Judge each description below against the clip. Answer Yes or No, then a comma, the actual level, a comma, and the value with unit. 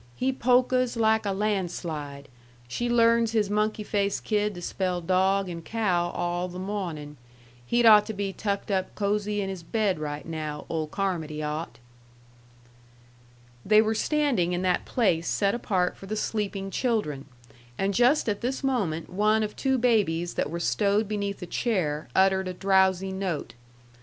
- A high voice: Yes, high, 195 Hz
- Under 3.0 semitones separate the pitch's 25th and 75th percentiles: No, average, 3.7 semitones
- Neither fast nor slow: Yes, average, 160 wpm